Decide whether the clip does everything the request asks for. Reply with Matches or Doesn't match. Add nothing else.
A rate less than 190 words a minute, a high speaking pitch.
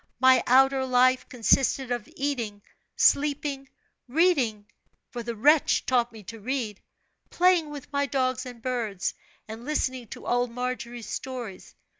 Matches